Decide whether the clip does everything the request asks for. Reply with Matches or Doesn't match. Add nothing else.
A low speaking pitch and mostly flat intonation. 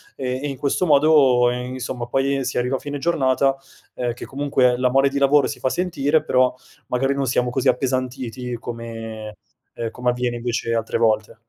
Matches